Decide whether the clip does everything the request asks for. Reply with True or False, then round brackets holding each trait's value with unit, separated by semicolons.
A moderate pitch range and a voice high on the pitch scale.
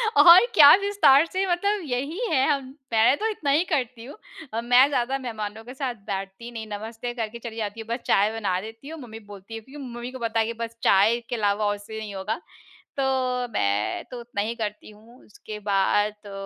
True (3.8 semitones; 235 Hz)